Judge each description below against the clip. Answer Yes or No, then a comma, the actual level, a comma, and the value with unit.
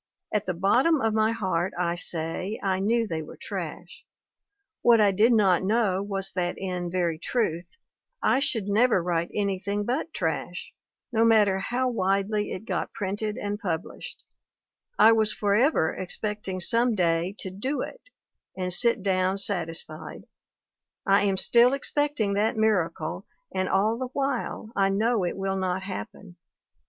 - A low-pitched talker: No, high, 200 Hz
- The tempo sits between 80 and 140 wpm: No, average, 150 wpm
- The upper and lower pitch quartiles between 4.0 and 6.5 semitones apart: No, average, 3.4 semitones